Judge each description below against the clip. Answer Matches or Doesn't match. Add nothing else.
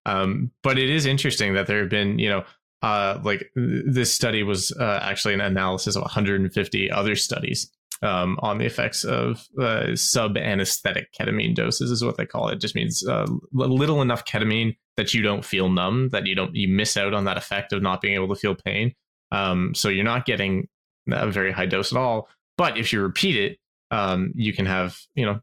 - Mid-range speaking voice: Doesn't match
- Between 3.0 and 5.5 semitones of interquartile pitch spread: Matches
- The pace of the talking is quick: Matches